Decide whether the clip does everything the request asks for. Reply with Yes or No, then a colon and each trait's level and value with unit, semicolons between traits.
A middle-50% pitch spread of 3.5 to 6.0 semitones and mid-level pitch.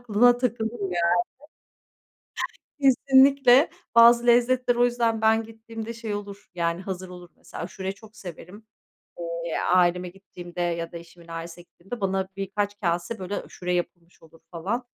No: average, 4.9 semitones; high, 200 Hz